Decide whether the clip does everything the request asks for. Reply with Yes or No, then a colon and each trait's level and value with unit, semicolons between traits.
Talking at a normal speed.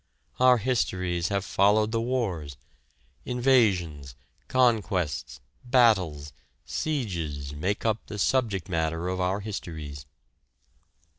No: slow, 95 wpm